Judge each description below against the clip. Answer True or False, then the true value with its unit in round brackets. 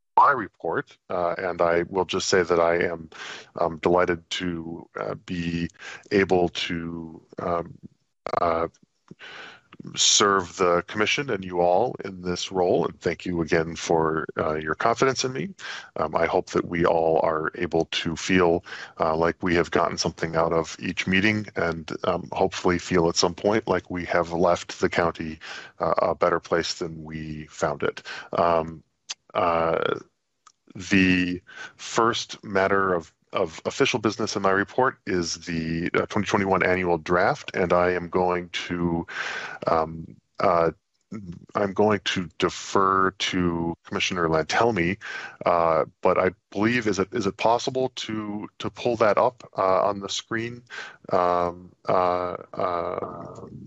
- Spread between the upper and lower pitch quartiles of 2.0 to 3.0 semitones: True (2.5 semitones)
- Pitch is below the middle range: True (90 Hz)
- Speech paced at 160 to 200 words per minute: False (150 wpm)